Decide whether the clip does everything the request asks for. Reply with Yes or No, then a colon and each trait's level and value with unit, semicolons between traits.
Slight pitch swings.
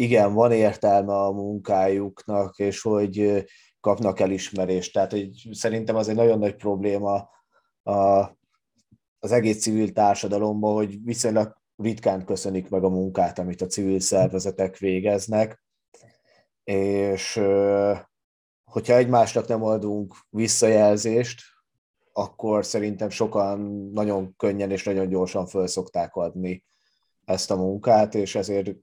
Yes: narrow, 1.9 semitones